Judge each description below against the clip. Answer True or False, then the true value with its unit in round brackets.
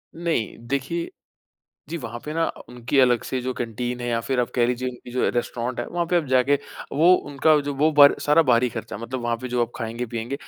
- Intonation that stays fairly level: False (3.1 semitones)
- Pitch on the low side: True (125 Hz)